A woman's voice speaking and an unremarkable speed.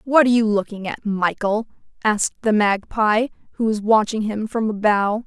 Yes: female; average, 180 wpm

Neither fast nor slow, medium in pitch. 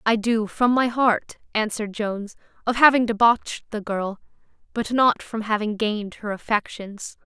No: average, 155 wpm; high, 220 Hz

